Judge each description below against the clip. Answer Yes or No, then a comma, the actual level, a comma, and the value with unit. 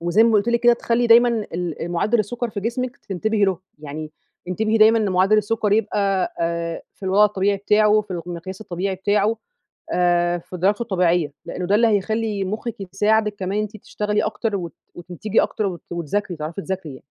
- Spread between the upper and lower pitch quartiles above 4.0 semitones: No, average, 3.5 semitones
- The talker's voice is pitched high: Yes, high, 200 Hz